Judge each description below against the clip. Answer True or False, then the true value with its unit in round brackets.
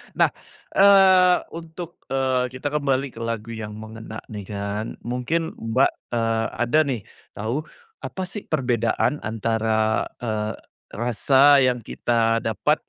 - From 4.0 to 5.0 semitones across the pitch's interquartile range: True (4.5 semitones)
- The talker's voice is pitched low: True (120 Hz)